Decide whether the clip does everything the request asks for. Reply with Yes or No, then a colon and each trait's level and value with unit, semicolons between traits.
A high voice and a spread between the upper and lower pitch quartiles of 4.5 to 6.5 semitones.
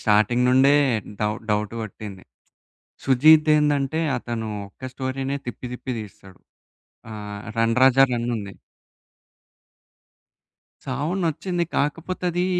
No: low, 125 Hz; average, 5.3 semitones